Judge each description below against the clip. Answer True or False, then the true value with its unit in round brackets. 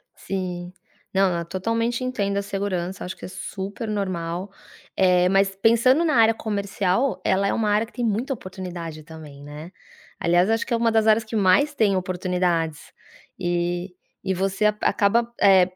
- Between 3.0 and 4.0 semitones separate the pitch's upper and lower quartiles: True (3.5 semitones)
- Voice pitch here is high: True (195 Hz)